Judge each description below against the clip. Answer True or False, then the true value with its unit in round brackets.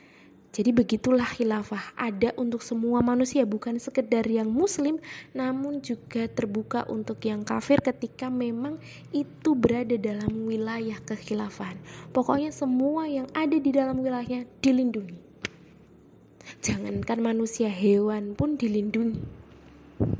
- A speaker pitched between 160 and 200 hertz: False (235 Hz)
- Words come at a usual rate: True (110 wpm)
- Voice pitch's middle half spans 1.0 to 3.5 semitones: True (3.1 semitones)